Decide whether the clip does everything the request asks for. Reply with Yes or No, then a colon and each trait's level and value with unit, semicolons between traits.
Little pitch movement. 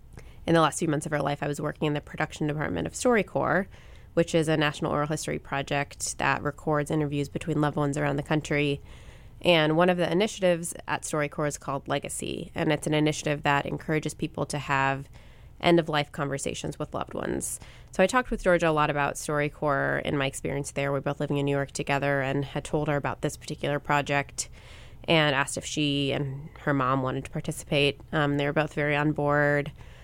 Yes: narrow, 1.7 semitones